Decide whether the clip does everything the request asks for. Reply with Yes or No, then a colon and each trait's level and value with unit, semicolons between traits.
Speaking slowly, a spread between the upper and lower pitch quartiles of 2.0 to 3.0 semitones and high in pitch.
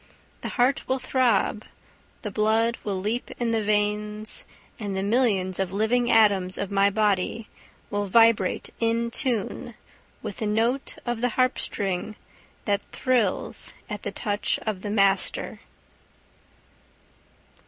Yes: slow, 130 wpm; narrow, 2.6 semitones; high, 215 Hz